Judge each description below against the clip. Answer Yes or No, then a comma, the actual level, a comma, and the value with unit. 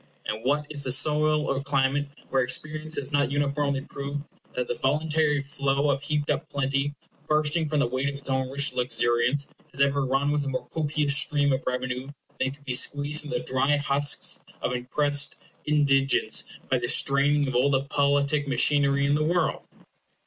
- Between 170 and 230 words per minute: Yes, average, 185 wpm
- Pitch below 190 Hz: Yes, medium, 140 Hz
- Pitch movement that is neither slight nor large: No, narrow, 1.6 semitones